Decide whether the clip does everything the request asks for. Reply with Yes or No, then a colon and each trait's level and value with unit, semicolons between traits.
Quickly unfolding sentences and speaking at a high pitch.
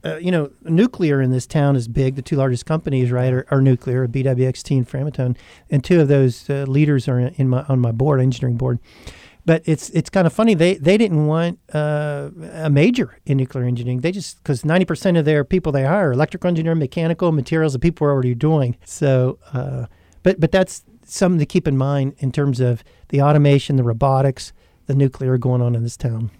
No: fast, 210 wpm; medium, 140 Hz